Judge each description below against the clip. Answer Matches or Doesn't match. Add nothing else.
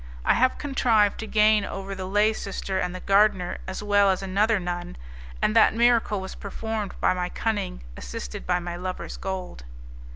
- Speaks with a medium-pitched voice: Doesn't match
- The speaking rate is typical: Matches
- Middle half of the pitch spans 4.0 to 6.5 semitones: Doesn't match